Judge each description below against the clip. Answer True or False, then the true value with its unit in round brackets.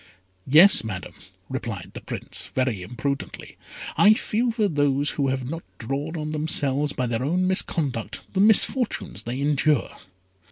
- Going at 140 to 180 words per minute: True (145 wpm)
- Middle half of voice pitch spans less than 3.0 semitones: False (4.7 semitones)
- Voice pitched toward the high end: False (145 Hz)